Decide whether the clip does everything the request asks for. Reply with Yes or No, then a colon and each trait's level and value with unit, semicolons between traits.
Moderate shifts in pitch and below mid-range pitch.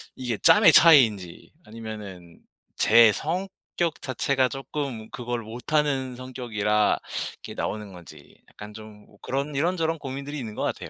Yes: average, 5.0 semitones; low, 125 Hz